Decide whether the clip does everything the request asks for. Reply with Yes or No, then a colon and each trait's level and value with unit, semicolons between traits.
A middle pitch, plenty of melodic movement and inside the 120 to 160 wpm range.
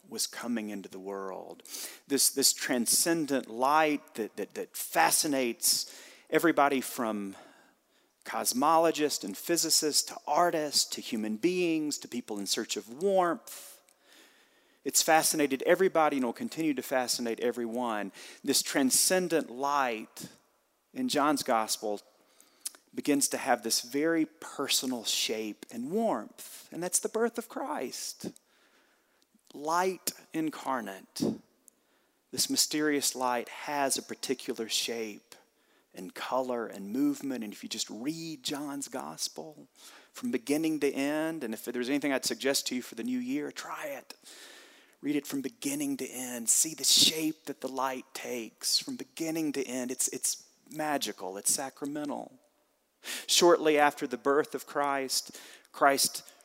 No: medium, 145 Hz; average, 4.5 semitones; slow, 135 wpm